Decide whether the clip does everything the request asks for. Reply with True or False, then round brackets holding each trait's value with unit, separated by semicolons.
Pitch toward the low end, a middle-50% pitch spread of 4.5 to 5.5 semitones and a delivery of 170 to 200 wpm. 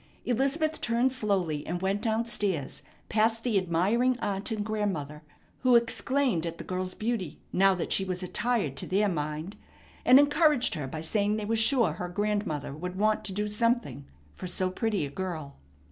False (205 Hz; 4.8 semitones; 175 wpm)